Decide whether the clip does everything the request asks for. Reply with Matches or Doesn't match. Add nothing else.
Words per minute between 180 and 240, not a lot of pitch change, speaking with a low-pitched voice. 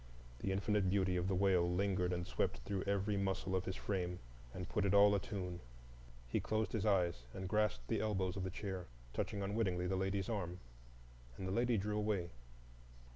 Matches